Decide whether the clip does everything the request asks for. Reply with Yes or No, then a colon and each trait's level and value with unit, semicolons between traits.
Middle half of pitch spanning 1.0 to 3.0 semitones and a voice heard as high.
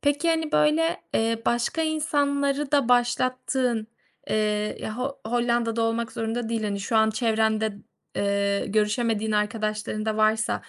No: average, 3.7 semitones; high, 230 Hz